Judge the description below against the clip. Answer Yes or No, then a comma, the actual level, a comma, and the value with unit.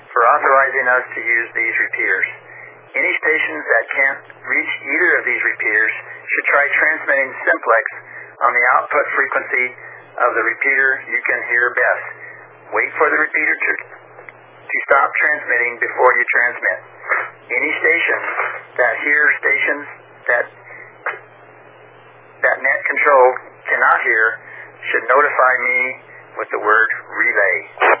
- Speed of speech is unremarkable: No, slow, 130 wpm